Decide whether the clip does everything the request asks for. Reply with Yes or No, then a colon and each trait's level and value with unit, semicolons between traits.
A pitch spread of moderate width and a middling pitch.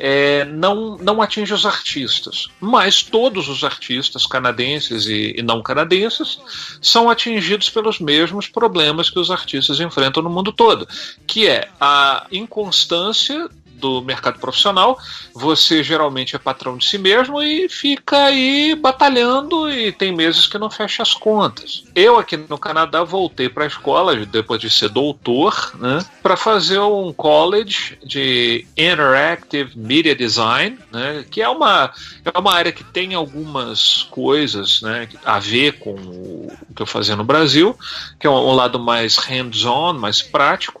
No: wide, 8.3 semitones; medium, 160 Hz